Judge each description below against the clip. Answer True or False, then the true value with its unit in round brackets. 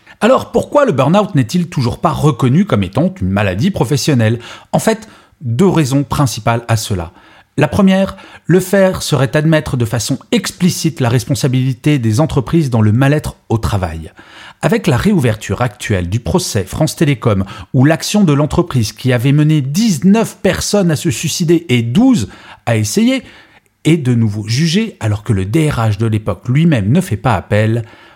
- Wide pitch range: True (6.5 semitones)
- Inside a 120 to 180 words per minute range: True (165 wpm)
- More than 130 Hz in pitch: True (140 Hz)